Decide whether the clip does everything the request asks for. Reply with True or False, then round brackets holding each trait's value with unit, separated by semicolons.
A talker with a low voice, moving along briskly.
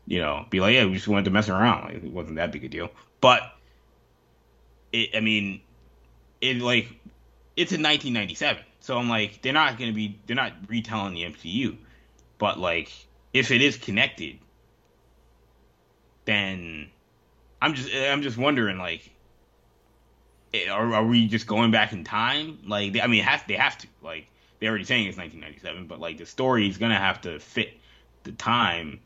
False (105 Hz; 175 wpm)